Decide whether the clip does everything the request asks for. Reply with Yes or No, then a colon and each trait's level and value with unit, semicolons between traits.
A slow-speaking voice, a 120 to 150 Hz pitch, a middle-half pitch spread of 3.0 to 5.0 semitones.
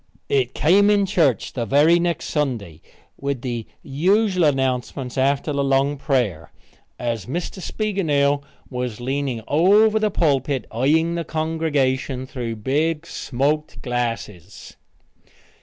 Yes: slow, 120 wpm; medium, 140 Hz; average, 4.5 semitones